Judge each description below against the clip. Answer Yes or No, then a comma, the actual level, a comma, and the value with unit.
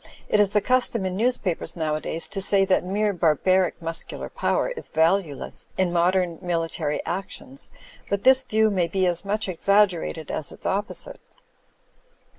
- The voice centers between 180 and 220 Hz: Yes, medium, 185 Hz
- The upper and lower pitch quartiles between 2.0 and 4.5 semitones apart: Yes, average, 3.7 semitones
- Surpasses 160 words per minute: No, average, 155 wpm